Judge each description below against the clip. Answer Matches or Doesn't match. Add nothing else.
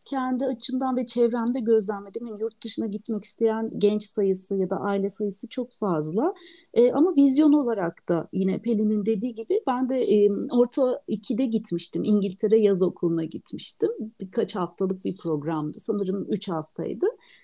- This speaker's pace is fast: Matches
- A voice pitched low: Doesn't match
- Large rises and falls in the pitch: Doesn't match